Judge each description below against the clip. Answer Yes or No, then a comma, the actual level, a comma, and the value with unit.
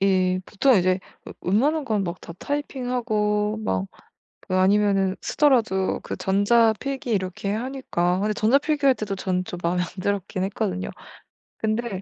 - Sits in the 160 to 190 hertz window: No, high, 205 Hz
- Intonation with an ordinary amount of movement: Yes, average, 4.4 semitones